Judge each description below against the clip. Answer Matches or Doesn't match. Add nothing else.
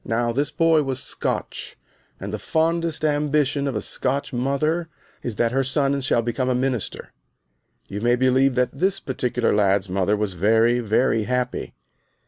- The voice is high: Doesn't match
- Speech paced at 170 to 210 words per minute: Doesn't match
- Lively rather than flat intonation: Doesn't match